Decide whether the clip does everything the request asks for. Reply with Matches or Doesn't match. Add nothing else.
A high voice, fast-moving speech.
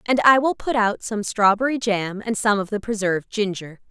Matches